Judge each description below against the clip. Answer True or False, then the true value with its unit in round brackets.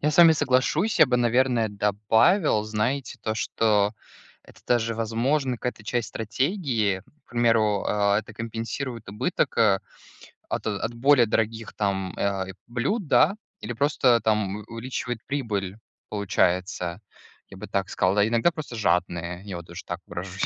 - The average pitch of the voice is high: False (110 Hz)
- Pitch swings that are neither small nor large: True (3.9 semitones)